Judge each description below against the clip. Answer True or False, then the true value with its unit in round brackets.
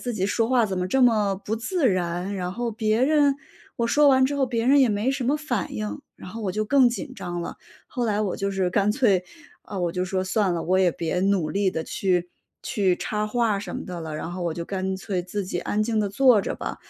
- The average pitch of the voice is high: True (205 Hz)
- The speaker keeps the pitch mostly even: False (4.6 semitones)